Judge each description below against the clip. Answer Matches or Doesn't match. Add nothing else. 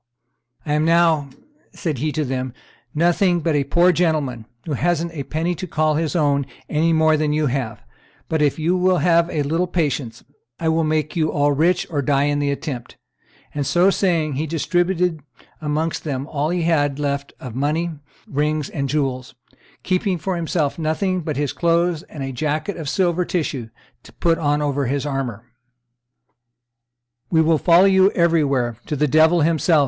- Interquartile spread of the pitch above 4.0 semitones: Doesn't match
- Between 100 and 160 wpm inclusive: Doesn't match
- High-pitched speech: Doesn't match